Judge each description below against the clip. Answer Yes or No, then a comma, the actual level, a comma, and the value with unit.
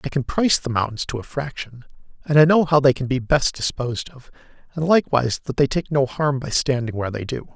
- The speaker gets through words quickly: Yes, fast, 240 wpm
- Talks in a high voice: No, low, 135 Hz